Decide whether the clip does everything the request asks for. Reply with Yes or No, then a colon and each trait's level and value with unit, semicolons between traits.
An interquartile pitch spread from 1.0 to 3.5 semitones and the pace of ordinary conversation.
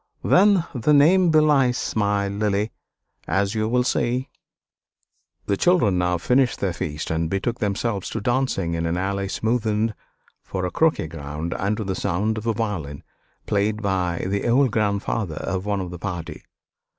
No: average, 4.5 semitones; average, 160 wpm